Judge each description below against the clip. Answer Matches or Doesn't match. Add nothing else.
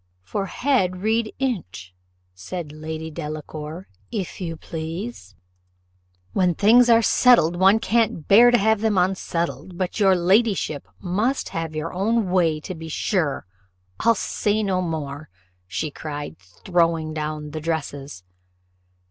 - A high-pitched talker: Doesn't match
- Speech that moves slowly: Matches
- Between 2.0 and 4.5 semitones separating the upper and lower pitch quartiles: Doesn't match